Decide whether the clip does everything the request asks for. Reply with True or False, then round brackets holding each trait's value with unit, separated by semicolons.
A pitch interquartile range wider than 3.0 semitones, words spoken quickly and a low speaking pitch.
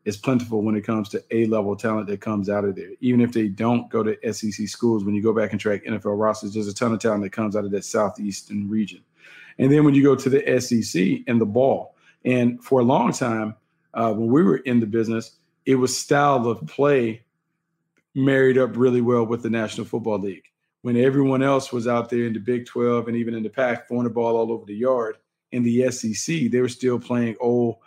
False (2.6 semitones; 235 wpm; 115 Hz)